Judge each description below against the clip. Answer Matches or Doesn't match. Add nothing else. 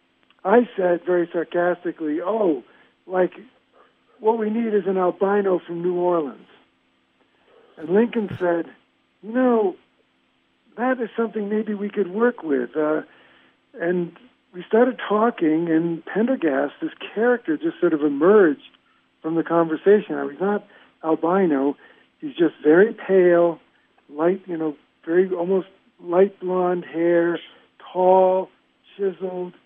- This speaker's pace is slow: Matches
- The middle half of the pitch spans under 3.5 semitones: Doesn't match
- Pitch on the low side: Doesn't match